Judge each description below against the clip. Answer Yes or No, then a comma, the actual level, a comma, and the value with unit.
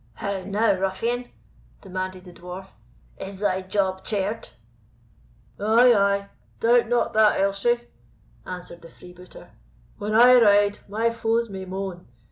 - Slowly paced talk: Yes, slow, 125 wpm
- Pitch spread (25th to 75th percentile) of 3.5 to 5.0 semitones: No, average, 3.1 semitones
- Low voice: No, high, 200 Hz